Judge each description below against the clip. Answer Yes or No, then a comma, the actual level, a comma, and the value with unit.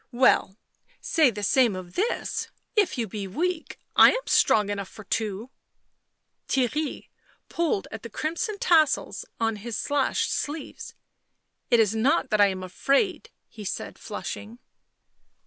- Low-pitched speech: No, high, 230 Hz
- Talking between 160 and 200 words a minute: No, average, 145 wpm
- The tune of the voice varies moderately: No, wide, 6.5 semitones